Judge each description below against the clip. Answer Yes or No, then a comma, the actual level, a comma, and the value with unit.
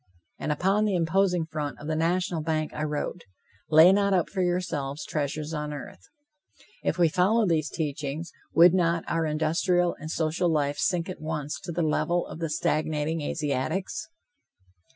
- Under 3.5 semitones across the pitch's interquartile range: Yes, average, 2.7 semitones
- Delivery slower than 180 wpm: Yes, average, 165 wpm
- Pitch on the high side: No, medium, 160 Hz